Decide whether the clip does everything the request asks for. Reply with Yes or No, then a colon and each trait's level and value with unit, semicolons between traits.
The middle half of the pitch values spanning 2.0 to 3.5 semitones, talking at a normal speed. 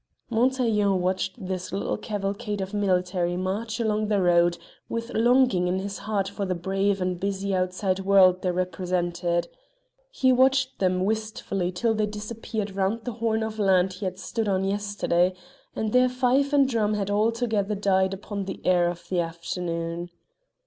Yes: average, 3.1 semitones; average, 165 wpm